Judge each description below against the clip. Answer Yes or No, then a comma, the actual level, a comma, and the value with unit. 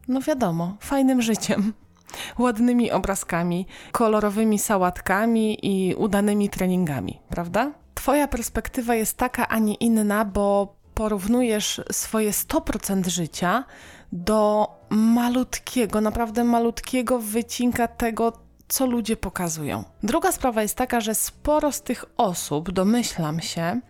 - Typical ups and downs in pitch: Yes, average, 3.6 semitones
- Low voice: No, high, 220 Hz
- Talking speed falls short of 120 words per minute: Yes, slow, 110 wpm